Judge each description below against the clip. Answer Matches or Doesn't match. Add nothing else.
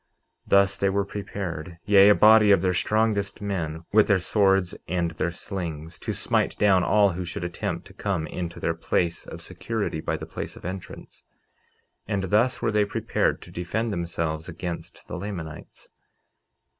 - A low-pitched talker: Matches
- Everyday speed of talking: Matches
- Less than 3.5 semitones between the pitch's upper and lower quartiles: Matches